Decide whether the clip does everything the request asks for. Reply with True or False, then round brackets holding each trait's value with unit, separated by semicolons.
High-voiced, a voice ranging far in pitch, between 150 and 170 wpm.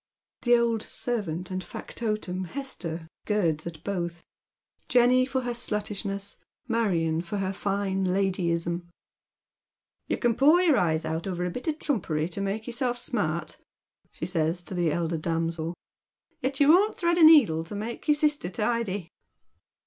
True (195 Hz; 6.1 semitones; 160 wpm)